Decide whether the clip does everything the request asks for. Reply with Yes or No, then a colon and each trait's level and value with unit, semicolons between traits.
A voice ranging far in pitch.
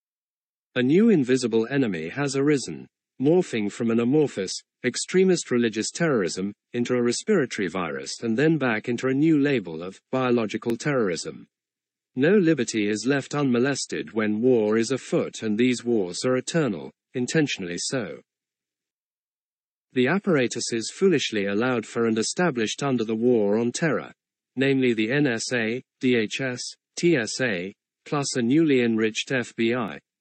No: average, 3.4 semitones